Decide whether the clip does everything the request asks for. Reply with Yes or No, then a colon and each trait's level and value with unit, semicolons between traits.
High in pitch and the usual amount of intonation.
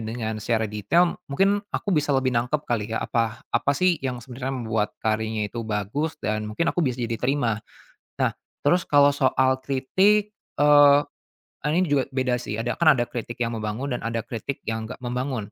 No: low, 125 Hz; average, 4.4 semitones